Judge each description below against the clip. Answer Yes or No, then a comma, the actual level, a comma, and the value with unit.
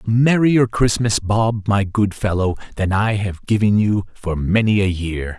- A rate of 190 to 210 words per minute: No, average, 180 wpm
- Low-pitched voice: Yes, low, 105 Hz